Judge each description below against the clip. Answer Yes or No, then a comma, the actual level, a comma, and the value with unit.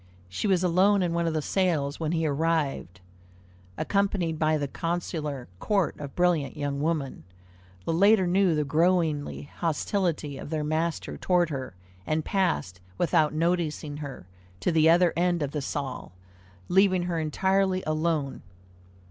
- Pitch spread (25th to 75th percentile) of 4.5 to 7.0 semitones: No, average, 3.3 semitones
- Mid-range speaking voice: Yes, medium, 165 Hz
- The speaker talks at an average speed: Yes, average, 150 wpm